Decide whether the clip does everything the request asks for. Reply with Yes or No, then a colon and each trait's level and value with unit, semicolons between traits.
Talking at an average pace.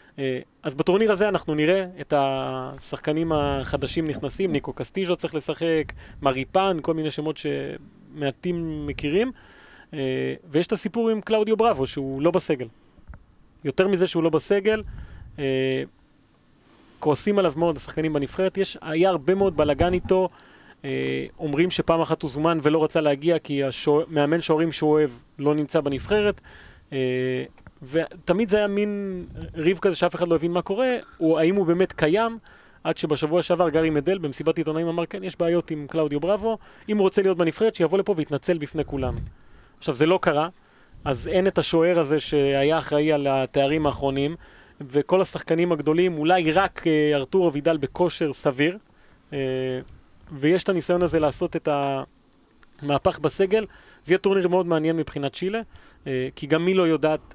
No: fast, 155 wpm